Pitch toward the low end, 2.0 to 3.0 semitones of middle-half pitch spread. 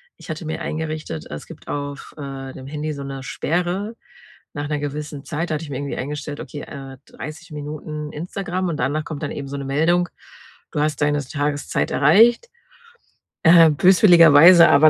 No: medium, 150 Hz; narrow, 2.5 semitones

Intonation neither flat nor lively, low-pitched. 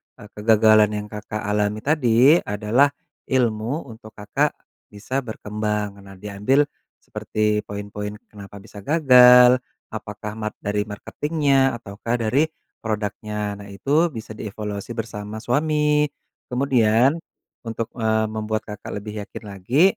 Yes: average, 3.2 semitones; low, 110 Hz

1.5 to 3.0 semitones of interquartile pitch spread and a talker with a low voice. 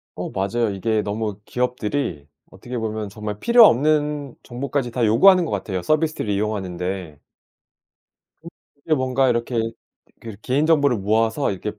No: average, 5.1 semitones; low, 115 Hz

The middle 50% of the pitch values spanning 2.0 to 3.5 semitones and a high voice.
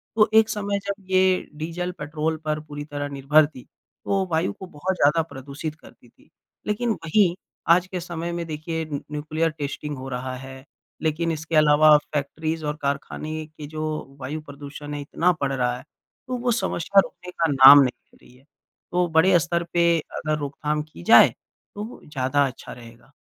No: average, 3.1 semitones; medium, 155 Hz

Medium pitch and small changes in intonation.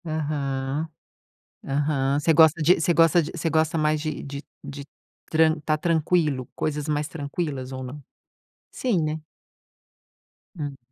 Yes: medium, 150 Hz; narrow, 2.1 semitones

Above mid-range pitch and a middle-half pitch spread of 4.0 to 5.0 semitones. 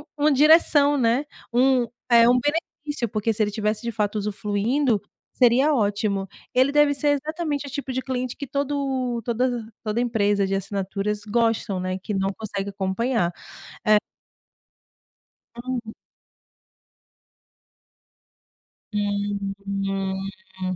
Yes: high, 230 Hz; average, 4.7 semitones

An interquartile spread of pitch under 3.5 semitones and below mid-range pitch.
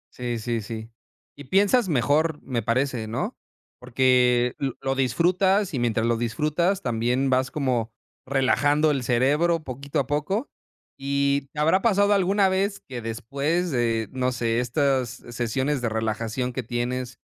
No: average, 4.0 semitones; low, 130 Hz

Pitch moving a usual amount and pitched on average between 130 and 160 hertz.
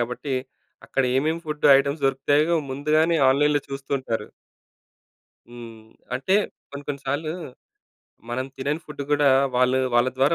No: narrow, 2.2 semitones; medium, 140 Hz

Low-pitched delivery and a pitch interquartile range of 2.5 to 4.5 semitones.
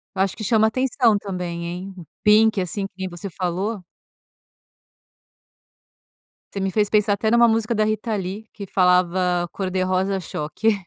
No: high, 195 Hz; average, 3.0 semitones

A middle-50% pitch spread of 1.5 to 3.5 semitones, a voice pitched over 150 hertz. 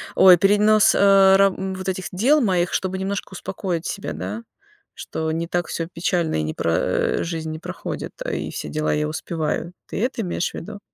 Yes: average, 3.1 semitones; medium, 185 Hz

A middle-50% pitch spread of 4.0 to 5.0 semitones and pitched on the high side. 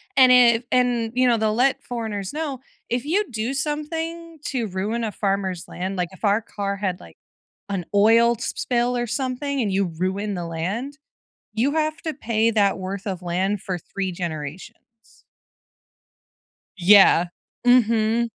Yes: average, 4.7 semitones; high, 225 Hz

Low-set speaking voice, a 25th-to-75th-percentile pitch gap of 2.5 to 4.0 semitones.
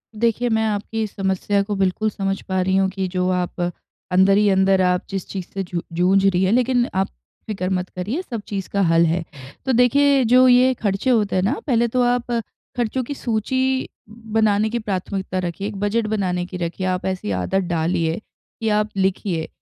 No: high, 200 Hz; average, 3.6 semitones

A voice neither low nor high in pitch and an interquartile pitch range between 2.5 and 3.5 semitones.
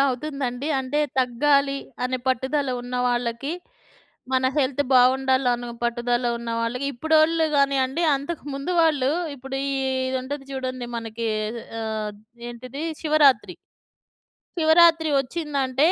No: very high, 265 Hz; average, 2.8 semitones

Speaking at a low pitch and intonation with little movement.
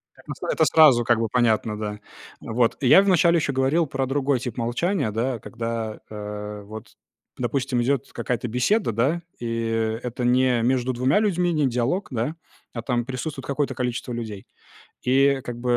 No: low, 125 Hz; average, 3.1 semitones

